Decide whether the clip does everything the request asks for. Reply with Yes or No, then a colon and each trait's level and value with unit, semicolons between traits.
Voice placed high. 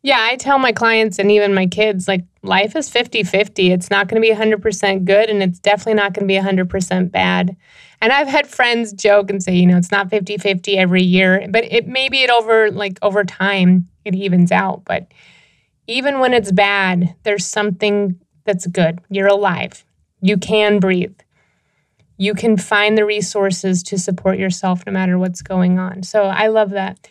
Yes: high, 200 Hz